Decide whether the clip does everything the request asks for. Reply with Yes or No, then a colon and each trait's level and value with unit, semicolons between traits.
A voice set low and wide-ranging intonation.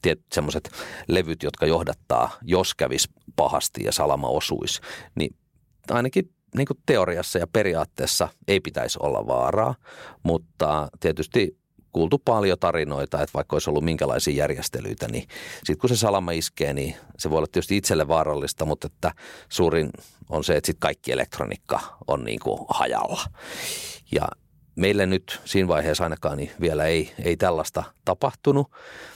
Yes: very low, 95 Hz; wide, 7.0 semitones